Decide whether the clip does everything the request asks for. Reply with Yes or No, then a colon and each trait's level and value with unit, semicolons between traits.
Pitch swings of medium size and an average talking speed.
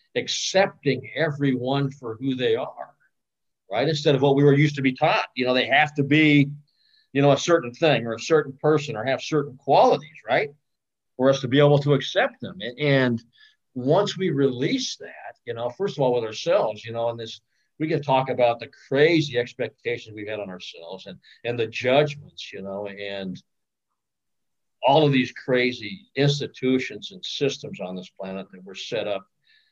Yes: average, 4.0 semitones; average, 185 wpm